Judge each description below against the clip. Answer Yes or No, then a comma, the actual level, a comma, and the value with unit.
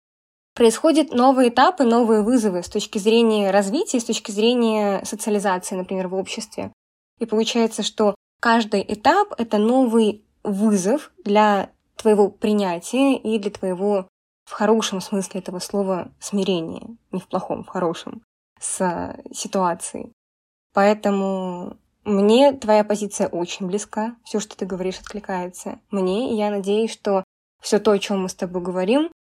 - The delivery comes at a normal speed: Yes, average, 140 wpm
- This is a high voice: Yes, high, 210 Hz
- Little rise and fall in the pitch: No, average, 3.0 semitones